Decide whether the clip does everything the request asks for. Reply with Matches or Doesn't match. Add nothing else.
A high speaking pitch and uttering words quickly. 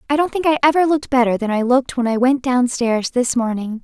Matches